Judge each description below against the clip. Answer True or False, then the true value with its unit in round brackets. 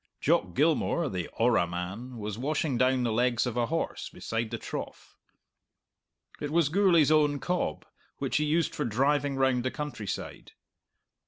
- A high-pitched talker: False (130 Hz)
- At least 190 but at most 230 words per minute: False (155 wpm)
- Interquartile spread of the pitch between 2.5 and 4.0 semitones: False (4.5 semitones)